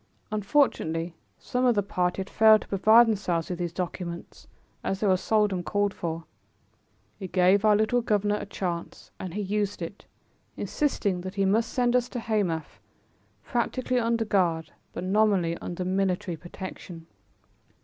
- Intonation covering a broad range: No, average, 3.4 semitones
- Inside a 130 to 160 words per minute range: Yes, average, 155 wpm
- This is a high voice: Yes, high, 195 Hz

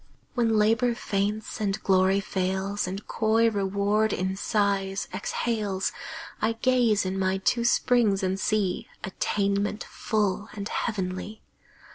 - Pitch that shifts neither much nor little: No, narrow, 2.1 semitones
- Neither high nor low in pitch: No, high, 205 Hz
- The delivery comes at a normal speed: No, slow, 120 wpm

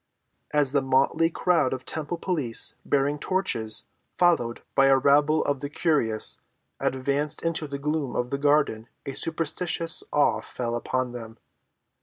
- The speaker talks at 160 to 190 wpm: No, average, 145 wpm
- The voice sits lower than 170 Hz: Yes, medium, 140 Hz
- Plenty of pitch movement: No, average, 3.4 semitones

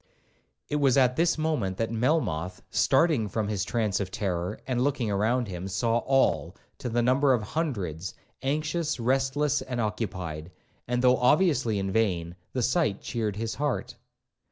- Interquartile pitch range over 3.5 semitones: Yes, average, 5.2 semitones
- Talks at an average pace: Yes, average, 155 wpm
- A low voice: Yes, low, 120 Hz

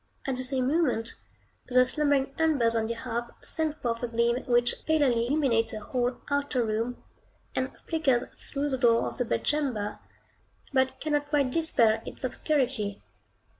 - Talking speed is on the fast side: No, average, 155 wpm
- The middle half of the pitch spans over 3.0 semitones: Yes, average, 3.5 semitones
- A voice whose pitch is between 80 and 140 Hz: No, very high, 255 Hz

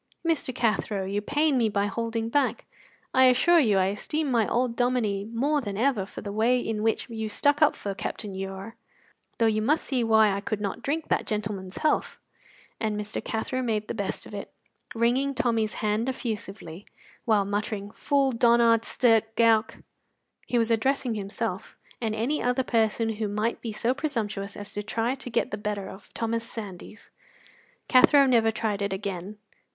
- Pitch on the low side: No, high, 225 Hz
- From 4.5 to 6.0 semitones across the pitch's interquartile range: No, average, 3.1 semitones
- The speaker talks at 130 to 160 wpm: No, average, 175 wpm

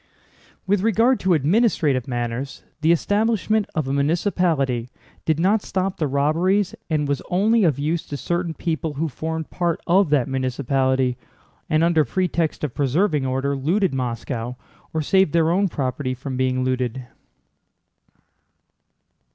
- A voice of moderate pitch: Yes, medium, 155 Hz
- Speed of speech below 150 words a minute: Yes, average, 140 wpm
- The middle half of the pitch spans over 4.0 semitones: Yes, wide, 5.4 semitones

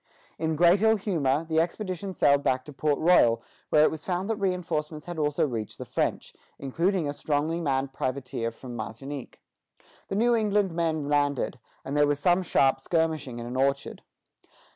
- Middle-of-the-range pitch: Yes, medium, 150 Hz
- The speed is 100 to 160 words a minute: No, average, 175 wpm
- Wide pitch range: No, average, 4.3 semitones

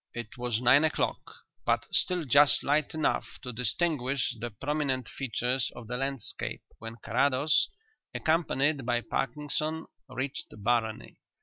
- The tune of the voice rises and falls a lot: No, average, 3.5 semitones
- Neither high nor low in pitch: No, low, 130 Hz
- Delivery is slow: Yes, slow, 125 wpm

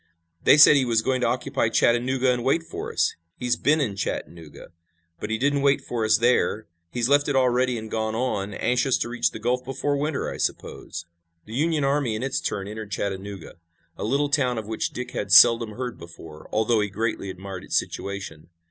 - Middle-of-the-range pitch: No, low, 120 Hz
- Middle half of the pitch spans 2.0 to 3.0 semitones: No, average, 3.9 semitones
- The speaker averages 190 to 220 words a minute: Yes, average, 200 wpm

